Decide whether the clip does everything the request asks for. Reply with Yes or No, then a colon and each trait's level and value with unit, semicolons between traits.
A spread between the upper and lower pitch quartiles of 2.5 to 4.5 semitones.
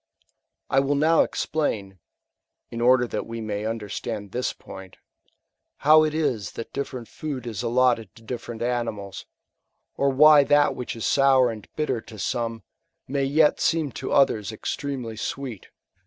Yes: average, 3.8 semitones